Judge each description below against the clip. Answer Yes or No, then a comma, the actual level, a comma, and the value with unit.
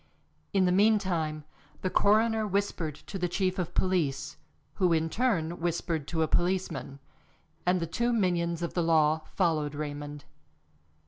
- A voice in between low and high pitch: Yes, medium, 175 Hz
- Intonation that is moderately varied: Yes, average, 3.2 semitones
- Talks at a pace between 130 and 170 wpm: Yes, average, 145 wpm